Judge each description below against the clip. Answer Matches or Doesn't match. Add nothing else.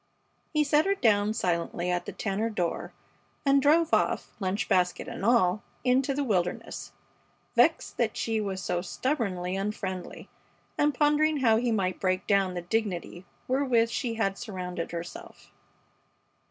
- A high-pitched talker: Matches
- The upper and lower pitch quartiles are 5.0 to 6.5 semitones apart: Matches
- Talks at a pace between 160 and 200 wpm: Doesn't match